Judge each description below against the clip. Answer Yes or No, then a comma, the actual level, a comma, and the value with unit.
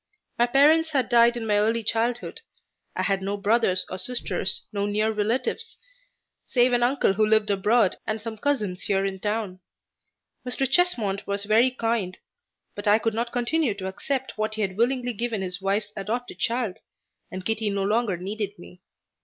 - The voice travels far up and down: No, average, 3.3 semitones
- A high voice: Yes, high, 220 Hz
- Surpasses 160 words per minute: Yes, average, 175 wpm